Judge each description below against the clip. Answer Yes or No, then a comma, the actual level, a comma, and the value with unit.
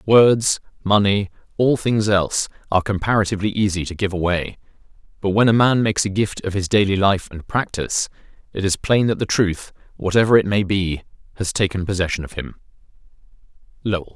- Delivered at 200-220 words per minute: No, average, 170 wpm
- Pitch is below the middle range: Yes, low, 100 Hz